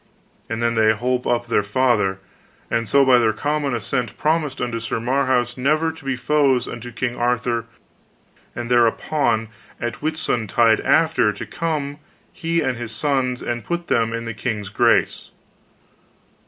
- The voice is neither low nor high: No, low, 120 Hz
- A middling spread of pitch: Yes, average, 3.2 semitones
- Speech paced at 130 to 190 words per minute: Yes, average, 155 wpm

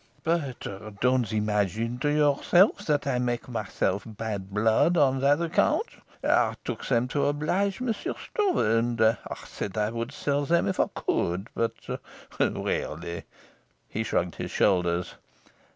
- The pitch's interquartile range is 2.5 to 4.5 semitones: No, wide, 5.5 semitones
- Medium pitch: No, low, 120 Hz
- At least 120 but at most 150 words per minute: Yes, average, 145 wpm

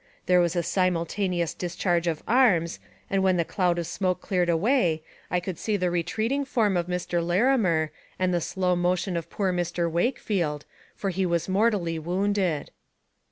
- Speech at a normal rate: Yes, average, 165 wpm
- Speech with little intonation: Yes, narrow, 2.3 semitones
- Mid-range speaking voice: Yes, medium, 180 Hz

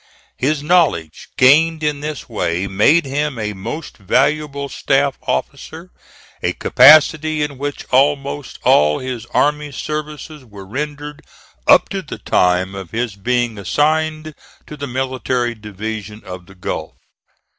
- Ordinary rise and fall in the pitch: No, wide, 5.7 semitones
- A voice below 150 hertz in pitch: Yes, low, 135 Hz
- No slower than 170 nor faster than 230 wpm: No, slow, 135 wpm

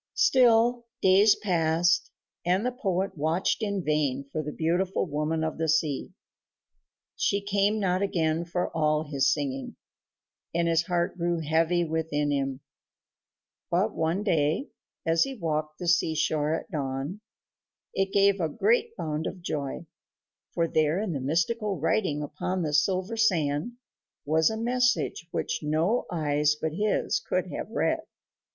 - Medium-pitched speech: Yes, medium, 165 Hz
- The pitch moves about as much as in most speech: Yes, average, 4.4 semitones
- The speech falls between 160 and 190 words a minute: No, average, 145 wpm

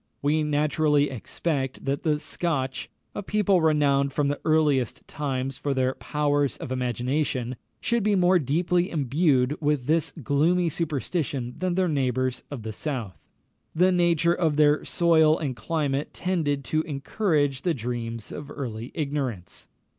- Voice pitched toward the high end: No, medium, 145 Hz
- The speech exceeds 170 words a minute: No, average, 145 wpm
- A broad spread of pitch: No, average, 3.7 semitones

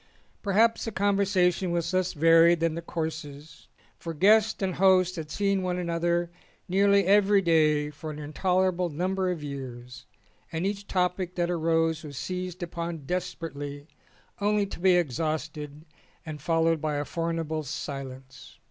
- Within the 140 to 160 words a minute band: Yes, average, 150 wpm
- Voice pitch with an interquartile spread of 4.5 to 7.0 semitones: No, average, 3.2 semitones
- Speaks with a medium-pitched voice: Yes, medium, 170 Hz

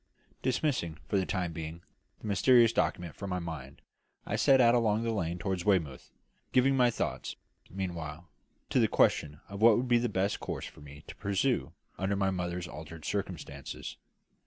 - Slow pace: No, average, 175 wpm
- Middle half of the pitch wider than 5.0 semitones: Yes, wide, 5.4 semitones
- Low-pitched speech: Yes, very low, 95 Hz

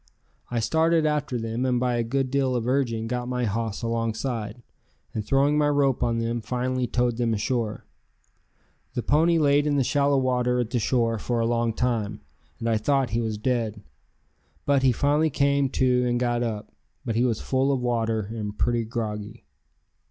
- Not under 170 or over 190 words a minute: Yes, average, 185 wpm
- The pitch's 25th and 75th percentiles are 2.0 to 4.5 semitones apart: Yes, average, 2.8 semitones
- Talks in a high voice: No, low, 120 Hz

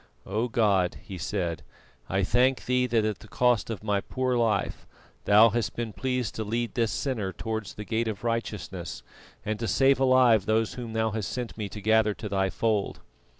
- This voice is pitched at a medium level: No, low, 110 Hz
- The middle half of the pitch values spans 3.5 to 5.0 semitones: No, narrow, 2.6 semitones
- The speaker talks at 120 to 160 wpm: No, average, 195 wpm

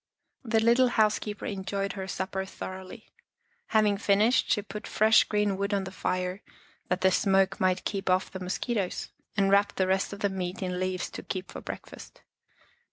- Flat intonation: Yes, narrow, 1.8 semitones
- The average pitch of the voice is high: Yes, high, 195 Hz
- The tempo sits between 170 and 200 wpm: Yes, average, 175 wpm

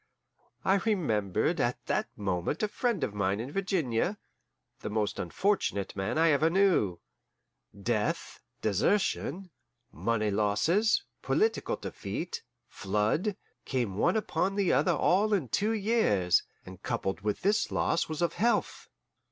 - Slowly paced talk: Yes, slow, 130 wpm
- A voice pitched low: No, medium, 155 Hz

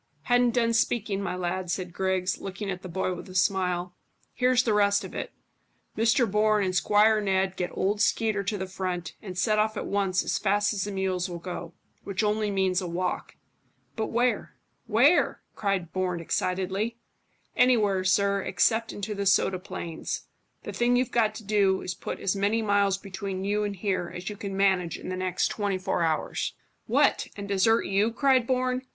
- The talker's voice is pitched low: No, high, 195 Hz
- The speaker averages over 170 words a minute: Yes, average, 190 wpm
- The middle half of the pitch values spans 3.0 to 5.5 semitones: No, narrow, 2.6 semitones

